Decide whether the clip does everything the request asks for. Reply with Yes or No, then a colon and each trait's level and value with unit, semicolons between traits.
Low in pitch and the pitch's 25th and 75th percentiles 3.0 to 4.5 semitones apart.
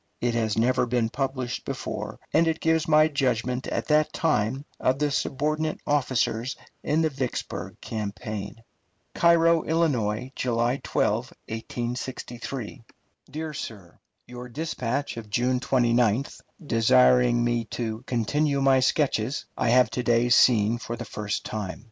Yes: low, 125 Hz; average, 3.7 semitones